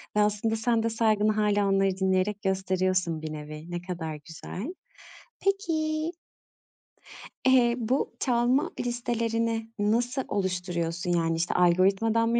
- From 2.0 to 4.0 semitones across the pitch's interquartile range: No, average, 4.5 semitones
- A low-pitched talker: No, high, 210 Hz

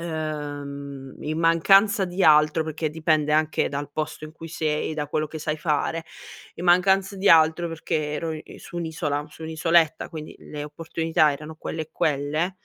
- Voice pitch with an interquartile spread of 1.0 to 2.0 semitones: Yes, narrow, 1.7 semitones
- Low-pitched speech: No, medium, 155 Hz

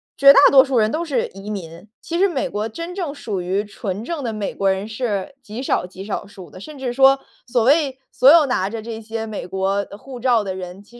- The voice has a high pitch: Yes, high, 225 Hz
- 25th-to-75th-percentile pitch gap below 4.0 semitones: No, average, 5.3 semitones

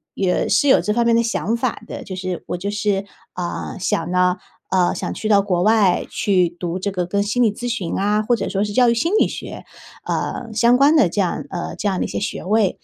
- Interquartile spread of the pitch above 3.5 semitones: Yes, average, 3.9 semitones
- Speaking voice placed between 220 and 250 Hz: No, high, 205 Hz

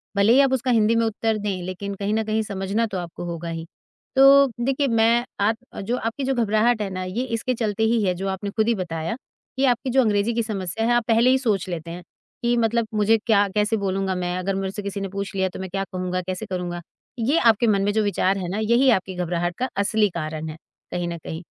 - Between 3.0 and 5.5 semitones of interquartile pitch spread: Yes, average, 3.7 semitones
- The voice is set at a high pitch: Yes, high, 205 Hz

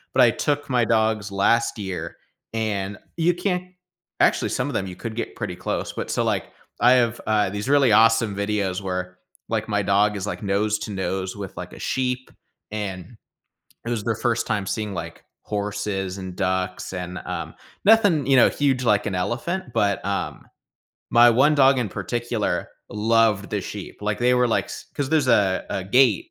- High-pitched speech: No, low, 105 Hz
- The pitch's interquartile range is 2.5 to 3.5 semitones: No, average, 4.0 semitones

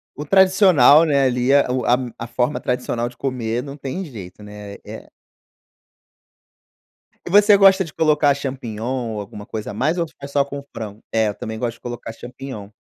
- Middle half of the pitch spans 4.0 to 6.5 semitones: Yes, average, 4.4 semitones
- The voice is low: Yes, low, 130 Hz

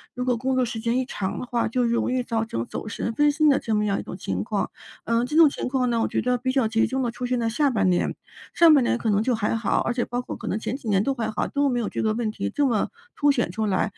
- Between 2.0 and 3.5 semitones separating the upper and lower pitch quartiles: Yes, average, 2.9 semitones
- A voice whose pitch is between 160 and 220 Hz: No, high, 235 Hz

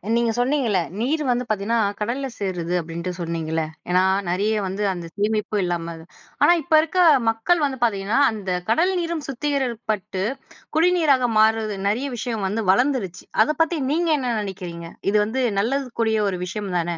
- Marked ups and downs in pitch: Yes, wide, 5.9 semitones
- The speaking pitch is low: No, high, 220 Hz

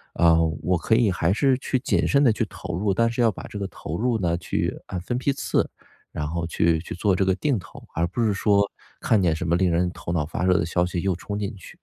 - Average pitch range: Yes, average, 4.3 semitones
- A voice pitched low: Yes, very low, 95 Hz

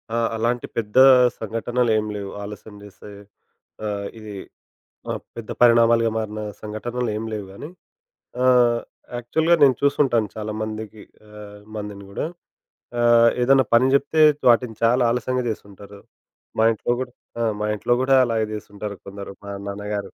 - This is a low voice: Yes, low, 110 Hz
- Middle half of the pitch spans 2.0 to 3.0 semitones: Yes, narrow, 2.6 semitones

